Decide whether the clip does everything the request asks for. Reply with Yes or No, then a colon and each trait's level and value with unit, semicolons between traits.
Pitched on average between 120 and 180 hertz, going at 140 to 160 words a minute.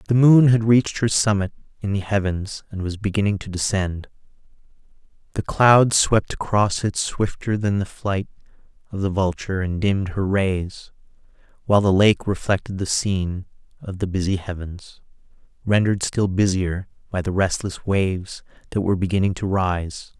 No: low, 100 Hz; average, 155 wpm